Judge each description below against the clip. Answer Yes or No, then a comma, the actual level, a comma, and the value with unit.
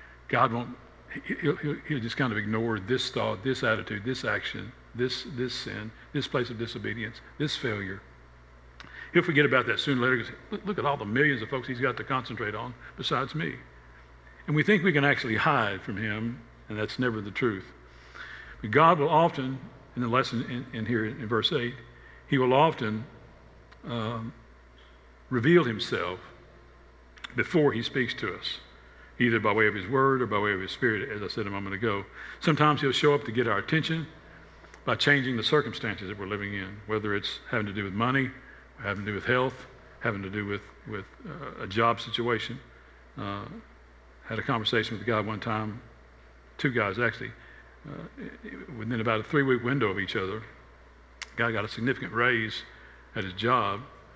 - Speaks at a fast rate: No, average, 190 wpm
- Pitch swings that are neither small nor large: Yes, average, 4.3 semitones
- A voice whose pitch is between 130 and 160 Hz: No, low, 115 Hz